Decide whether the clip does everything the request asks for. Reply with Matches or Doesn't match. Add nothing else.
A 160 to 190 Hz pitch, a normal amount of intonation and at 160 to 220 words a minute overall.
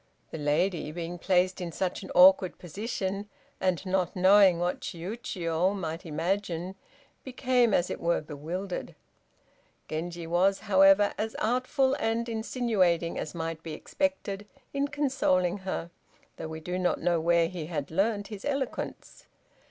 Doesn't match